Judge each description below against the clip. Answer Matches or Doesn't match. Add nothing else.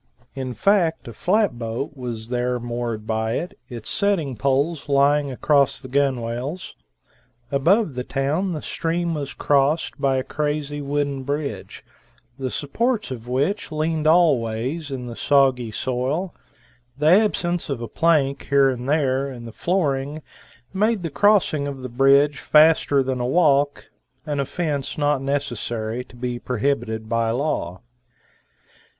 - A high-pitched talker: Doesn't match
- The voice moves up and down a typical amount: Matches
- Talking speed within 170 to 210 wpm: Doesn't match